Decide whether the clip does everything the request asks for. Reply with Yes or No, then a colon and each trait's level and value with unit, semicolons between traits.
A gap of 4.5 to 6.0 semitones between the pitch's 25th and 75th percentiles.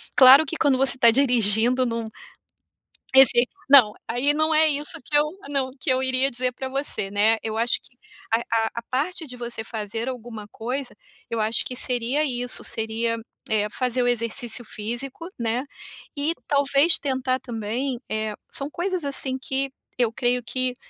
No: average, 3.0 semitones